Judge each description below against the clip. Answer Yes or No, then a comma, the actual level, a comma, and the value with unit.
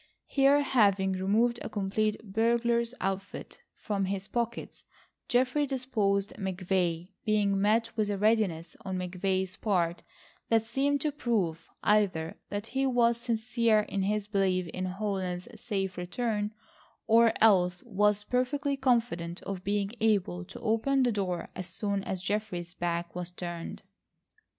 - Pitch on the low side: No, high, 205 Hz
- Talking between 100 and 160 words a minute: Yes, slow, 135 wpm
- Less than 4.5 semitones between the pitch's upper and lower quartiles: Yes, average, 3.9 semitones